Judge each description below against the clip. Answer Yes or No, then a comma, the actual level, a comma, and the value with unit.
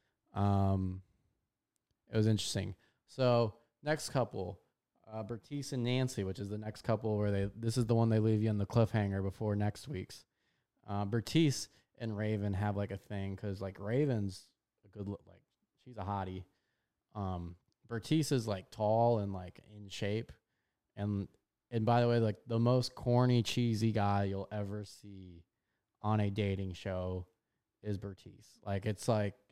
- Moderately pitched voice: No, low, 105 Hz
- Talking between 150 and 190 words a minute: Yes, average, 165 wpm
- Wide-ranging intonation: No, average, 2.9 semitones